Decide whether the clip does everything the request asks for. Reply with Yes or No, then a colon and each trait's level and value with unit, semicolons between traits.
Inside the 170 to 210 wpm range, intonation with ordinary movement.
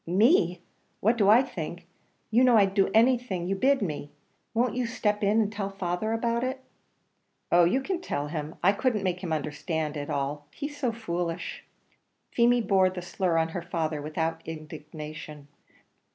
No: average, 175 wpm; wide, 6.2 semitones